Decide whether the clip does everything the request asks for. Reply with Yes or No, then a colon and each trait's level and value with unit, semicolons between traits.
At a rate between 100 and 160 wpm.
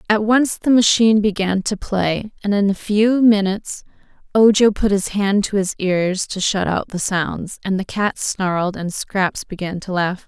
No: average, 195 wpm